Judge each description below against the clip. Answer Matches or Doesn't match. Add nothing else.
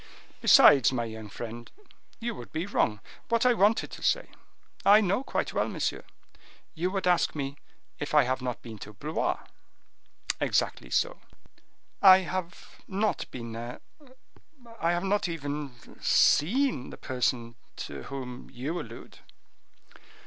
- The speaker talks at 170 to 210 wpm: Doesn't match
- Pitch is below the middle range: Doesn't match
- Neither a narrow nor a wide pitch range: Doesn't match